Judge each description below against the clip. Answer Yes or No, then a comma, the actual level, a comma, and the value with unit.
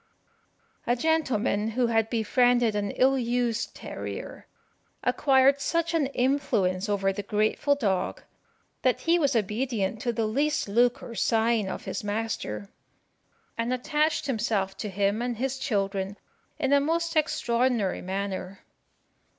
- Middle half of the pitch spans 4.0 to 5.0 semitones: Yes, average, 4.6 semitones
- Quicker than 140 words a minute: No, slow, 135 wpm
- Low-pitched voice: No, high, 235 Hz